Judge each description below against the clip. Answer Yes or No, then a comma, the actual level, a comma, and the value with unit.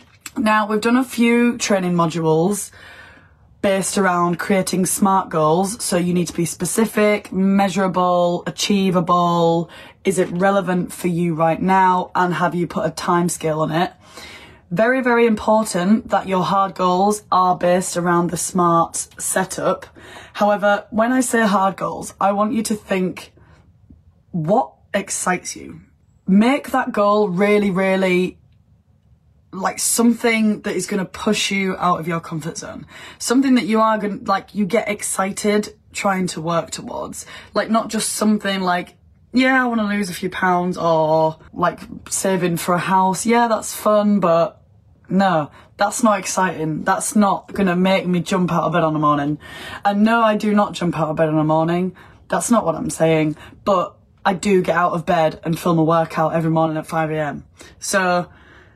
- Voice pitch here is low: No, medium, 185 Hz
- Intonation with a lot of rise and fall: No, average, 3.5 semitones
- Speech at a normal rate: Yes, average, 170 wpm